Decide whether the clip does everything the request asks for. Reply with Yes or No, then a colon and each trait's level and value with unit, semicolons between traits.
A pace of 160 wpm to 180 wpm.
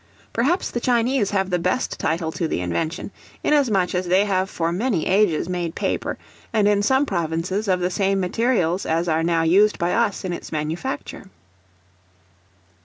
Yes: average, 170 wpm